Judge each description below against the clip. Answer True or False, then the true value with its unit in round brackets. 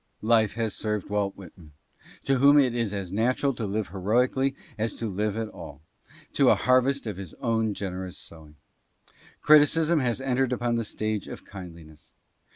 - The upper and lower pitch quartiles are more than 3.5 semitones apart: True (4.6 semitones)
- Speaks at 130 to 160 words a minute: False (170 wpm)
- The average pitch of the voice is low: True (110 Hz)